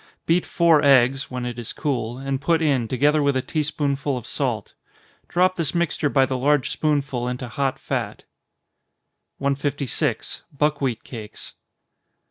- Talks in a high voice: No, medium, 140 Hz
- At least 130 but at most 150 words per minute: Yes, average, 145 wpm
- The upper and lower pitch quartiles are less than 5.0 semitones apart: Yes, average, 2.8 semitones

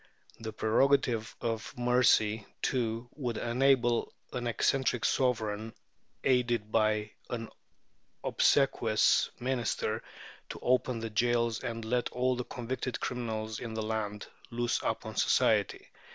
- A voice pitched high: No, low, 115 Hz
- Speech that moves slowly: Yes, slow, 115 wpm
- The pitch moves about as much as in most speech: No, narrow, 2.0 semitones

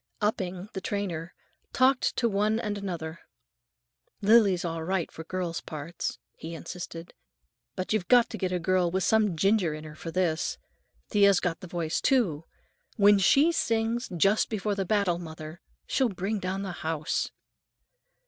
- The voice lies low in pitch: No, medium, 185 Hz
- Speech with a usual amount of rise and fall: Yes, average, 3.8 semitones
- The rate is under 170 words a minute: Yes, average, 160 wpm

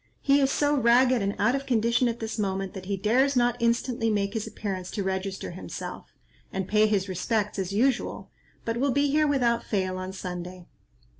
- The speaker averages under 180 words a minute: No, average, 195 wpm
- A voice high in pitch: Yes, high, 220 Hz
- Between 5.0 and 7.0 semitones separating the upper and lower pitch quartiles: No, average, 4.4 semitones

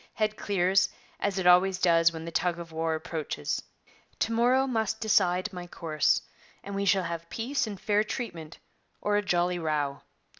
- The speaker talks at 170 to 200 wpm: Yes, average, 175 wpm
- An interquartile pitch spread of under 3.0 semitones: No, average, 3.8 semitones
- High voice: No, medium, 180 Hz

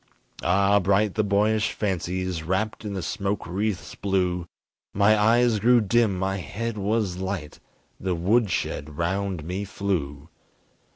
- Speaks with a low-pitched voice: Yes, low, 100 Hz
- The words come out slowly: Yes, slow, 130 wpm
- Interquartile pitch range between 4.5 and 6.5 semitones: No, average, 2.9 semitones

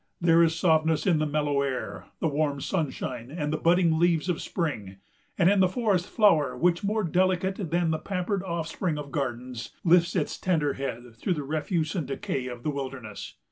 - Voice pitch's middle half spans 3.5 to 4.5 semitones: Yes, average, 4.1 semitones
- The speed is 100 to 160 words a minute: No, average, 185 wpm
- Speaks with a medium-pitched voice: Yes, medium, 160 Hz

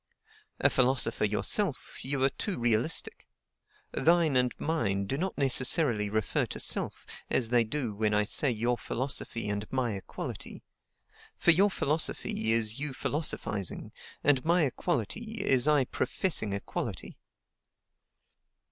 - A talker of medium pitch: No, low, 130 Hz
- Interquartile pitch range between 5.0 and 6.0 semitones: Yes, wide, 5.5 semitones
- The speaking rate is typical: No, slow, 130 wpm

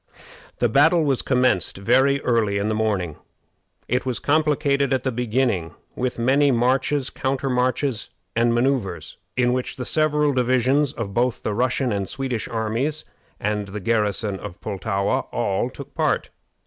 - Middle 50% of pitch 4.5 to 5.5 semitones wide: No, average, 3.9 semitones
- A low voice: Yes, low, 125 Hz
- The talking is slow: No, average, 150 wpm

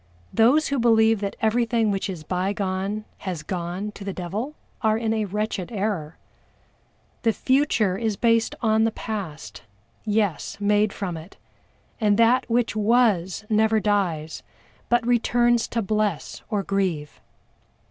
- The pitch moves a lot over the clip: No, average, 2.9 semitones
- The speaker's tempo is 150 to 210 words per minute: No, slow, 135 wpm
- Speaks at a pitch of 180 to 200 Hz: No, high, 210 Hz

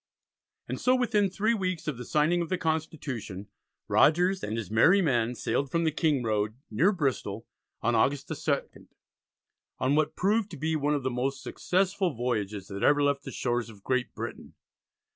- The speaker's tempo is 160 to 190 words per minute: Yes, average, 180 wpm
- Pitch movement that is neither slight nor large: No, wide, 6.4 semitones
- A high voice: No, medium, 145 Hz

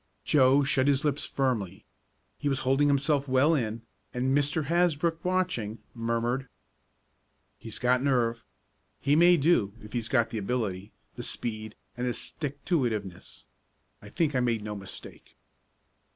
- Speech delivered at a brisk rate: No, average, 150 wpm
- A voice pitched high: No, low, 130 Hz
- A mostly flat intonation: No, average, 4.1 semitones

